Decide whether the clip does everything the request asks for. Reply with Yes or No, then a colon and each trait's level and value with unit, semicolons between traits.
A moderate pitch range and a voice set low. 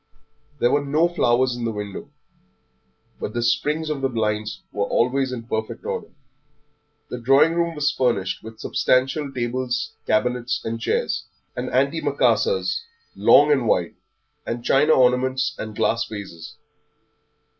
Yes: average, 3.9 semitones; low, 125 Hz